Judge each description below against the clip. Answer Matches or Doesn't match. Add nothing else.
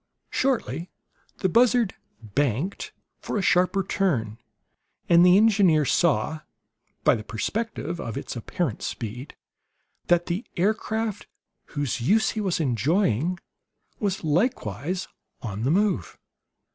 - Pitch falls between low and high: Matches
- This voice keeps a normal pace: Doesn't match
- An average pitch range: Doesn't match